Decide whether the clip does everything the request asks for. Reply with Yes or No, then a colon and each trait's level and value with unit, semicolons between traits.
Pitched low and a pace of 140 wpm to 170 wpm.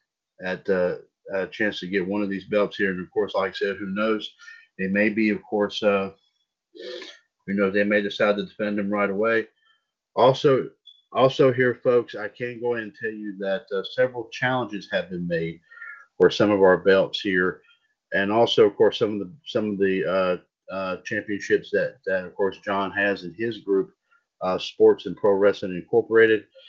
No: low, 110 Hz; average, 195 wpm